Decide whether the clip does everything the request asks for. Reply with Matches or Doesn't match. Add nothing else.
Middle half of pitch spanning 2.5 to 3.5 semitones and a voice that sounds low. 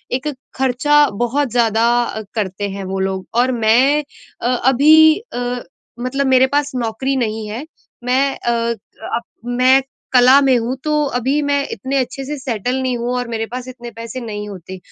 Doesn't match